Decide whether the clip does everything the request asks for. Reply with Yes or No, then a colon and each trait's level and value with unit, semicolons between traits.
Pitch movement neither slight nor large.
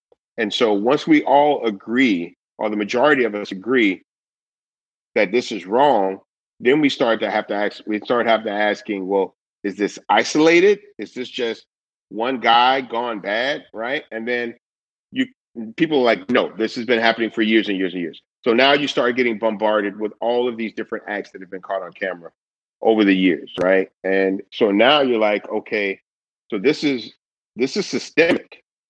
Yes: average, 3.5 semitones